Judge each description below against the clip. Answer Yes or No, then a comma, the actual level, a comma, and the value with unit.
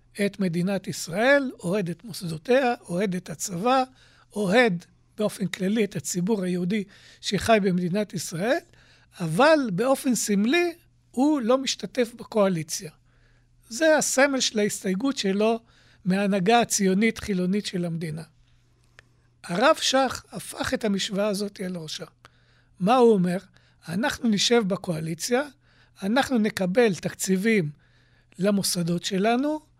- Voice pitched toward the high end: Yes, high, 200 Hz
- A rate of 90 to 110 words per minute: Yes, average, 105 wpm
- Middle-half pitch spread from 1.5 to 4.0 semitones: No, average, 5.2 semitones